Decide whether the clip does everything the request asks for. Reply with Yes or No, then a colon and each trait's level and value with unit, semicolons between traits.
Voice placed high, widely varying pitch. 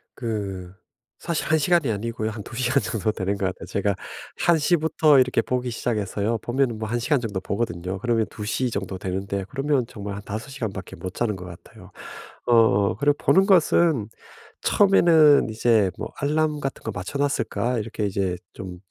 No: low, 115 Hz; wide, 5.8 semitones